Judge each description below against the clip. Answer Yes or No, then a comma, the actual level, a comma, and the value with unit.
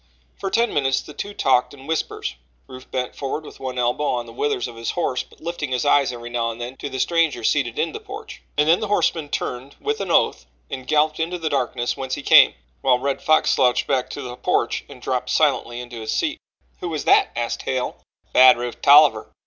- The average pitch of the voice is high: No, low, 135 Hz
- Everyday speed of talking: No, fast, 230 wpm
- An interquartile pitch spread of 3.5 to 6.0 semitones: Yes, average, 4.0 semitones